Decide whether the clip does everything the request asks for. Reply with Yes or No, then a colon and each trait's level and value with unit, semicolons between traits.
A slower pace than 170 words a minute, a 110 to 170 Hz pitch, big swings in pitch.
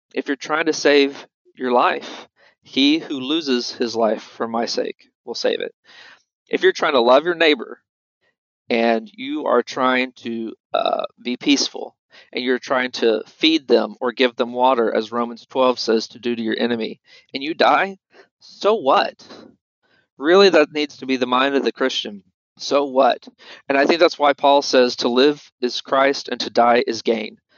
No: average, 185 wpm; medium, 140 Hz; wide, 7.9 semitones